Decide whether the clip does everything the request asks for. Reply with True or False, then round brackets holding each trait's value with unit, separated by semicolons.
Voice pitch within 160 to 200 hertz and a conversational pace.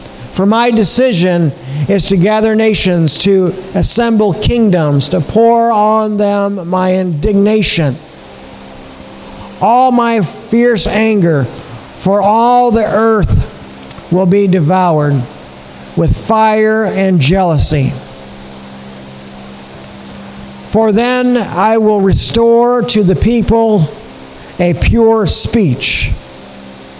False (185 Hz; 95 wpm)